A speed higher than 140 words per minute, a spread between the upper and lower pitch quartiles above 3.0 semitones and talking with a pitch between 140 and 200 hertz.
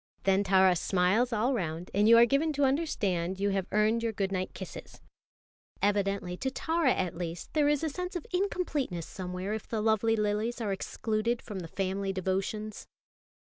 No: average, 180 wpm; average, 4.1 semitones; high, 210 Hz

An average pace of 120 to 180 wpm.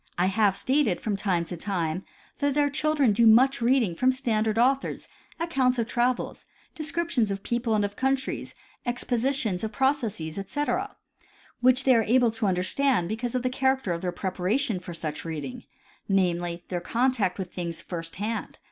Yes: average, 170 wpm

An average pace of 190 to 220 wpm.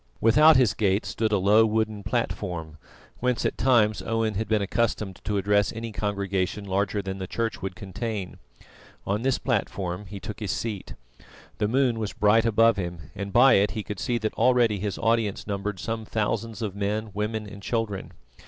No: average, 180 wpm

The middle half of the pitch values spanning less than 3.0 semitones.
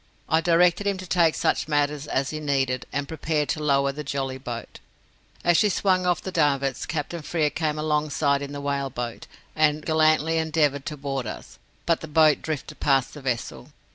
Yes: narrow, 2.5 semitones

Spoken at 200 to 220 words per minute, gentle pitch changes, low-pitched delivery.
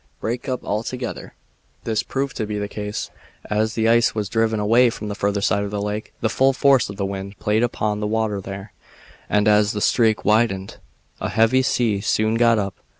Yes: fast, 205 wpm; narrow, 1.9 semitones; low, 110 Hz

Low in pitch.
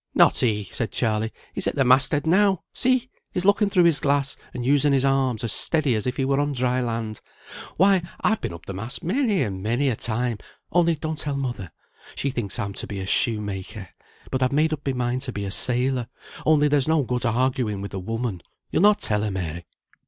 Yes: low, 130 Hz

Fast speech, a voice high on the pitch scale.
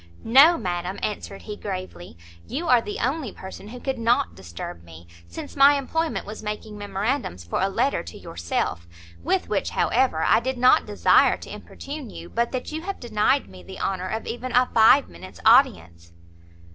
No: average, 180 wpm; high, 215 Hz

